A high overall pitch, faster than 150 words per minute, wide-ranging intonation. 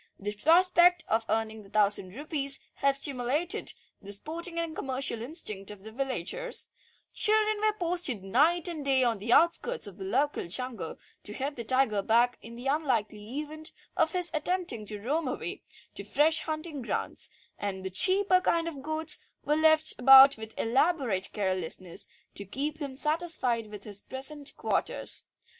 Yes: very high, 270 Hz; average, 160 wpm; wide, 6.8 semitones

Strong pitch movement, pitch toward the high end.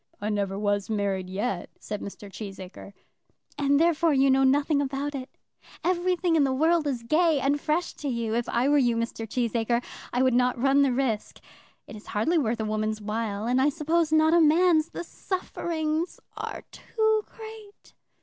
Yes: wide, 6.1 semitones; very high, 270 Hz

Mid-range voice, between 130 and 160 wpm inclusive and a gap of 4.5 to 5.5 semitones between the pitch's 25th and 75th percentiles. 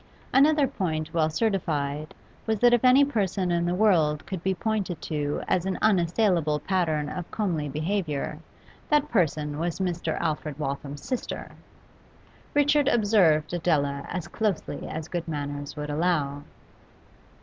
Yes: medium, 170 Hz; average, 140 wpm; average, 5.2 semitones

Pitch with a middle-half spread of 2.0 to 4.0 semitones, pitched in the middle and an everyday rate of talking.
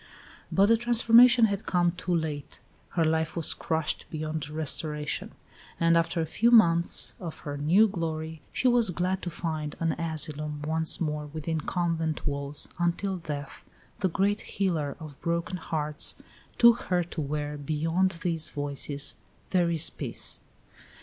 Yes: average, 3.0 semitones; medium, 165 Hz; average, 150 wpm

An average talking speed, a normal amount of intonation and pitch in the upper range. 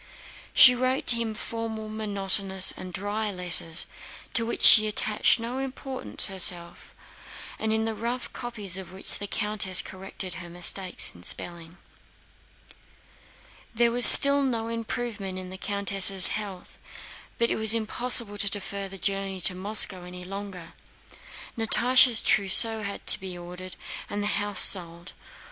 Yes: average, 145 wpm; average, 3.3 semitones; high, 205 Hz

